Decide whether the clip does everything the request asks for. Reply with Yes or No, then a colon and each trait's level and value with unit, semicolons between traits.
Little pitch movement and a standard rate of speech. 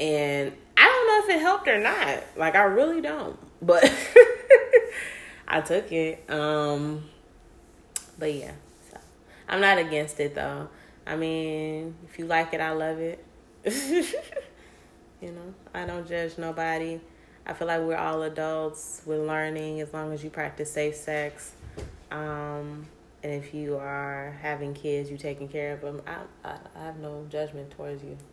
Yes: narrow, 2.0 semitones; average, 160 wpm